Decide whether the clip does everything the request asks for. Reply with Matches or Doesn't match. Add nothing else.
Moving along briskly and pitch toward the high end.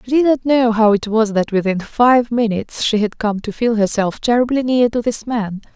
Matches